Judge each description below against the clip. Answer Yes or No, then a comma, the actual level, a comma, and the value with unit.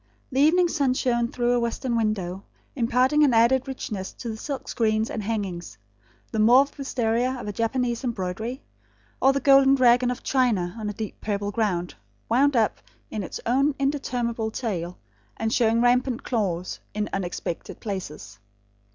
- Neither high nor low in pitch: No, high, 235 Hz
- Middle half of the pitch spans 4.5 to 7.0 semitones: No, average, 3.6 semitones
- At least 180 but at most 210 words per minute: No, average, 160 wpm